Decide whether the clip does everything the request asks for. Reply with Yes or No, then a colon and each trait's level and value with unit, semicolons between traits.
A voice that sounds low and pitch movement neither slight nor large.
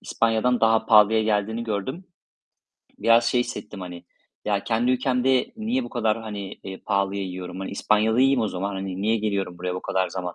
Yes: low, 110 Hz; average, 3.3 semitones